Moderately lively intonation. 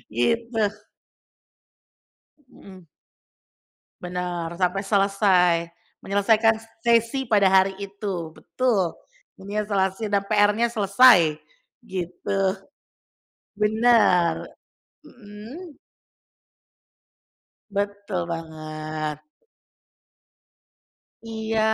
Yes: average, 3.6 semitones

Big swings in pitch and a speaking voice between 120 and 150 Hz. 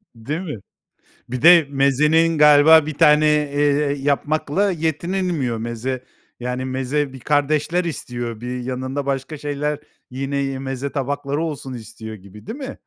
No: average, 3.0 semitones; medium, 140 Hz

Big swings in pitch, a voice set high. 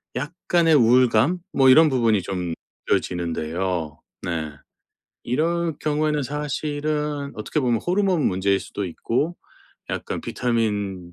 No: wide, 7.7 semitones; low, 125 Hz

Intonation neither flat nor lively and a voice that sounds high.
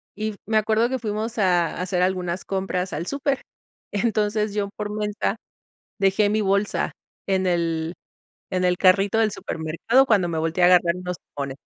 Yes: average, 3.1 semitones; high, 195 Hz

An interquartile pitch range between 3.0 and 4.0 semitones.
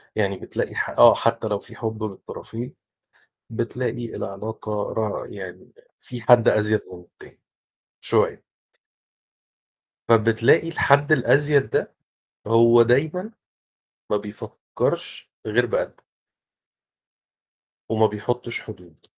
No: narrow, 2.6 semitones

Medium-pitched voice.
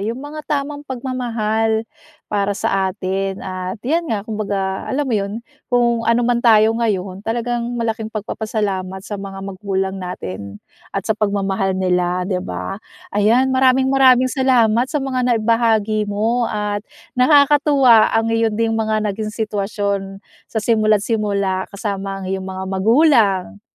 No: high, 215 Hz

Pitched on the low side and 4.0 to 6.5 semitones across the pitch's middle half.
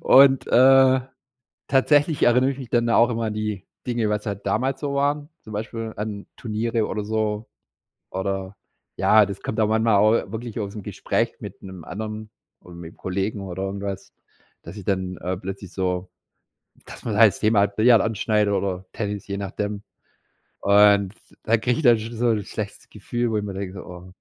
No: low, 105 Hz; average, 2.7 semitones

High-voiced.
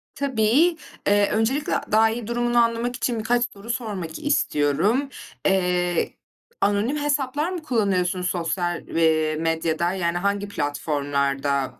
Yes: high, 205 Hz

